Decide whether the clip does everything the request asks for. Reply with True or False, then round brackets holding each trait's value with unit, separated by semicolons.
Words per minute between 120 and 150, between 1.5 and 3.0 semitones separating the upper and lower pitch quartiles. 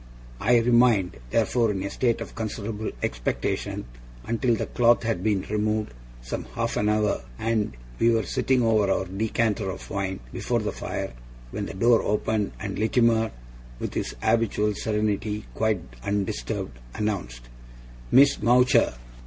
True (145 wpm; 2.5 semitones)